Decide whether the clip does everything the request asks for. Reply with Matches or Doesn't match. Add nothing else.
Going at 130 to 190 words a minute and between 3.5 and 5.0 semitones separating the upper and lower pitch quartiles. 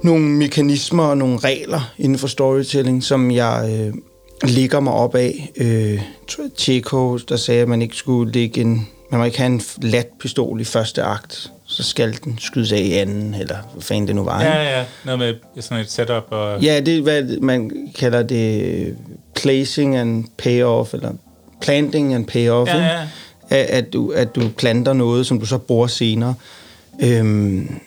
Doesn't match